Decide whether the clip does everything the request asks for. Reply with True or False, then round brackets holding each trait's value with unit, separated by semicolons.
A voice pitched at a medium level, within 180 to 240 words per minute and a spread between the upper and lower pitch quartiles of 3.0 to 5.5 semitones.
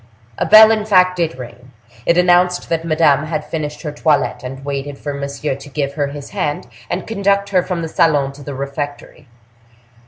True (150 Hz; 190 wpm; 4.2 semitones)